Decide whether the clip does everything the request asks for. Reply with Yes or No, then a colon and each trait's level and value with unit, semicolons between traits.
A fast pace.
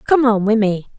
Yes: fast, 245 wpm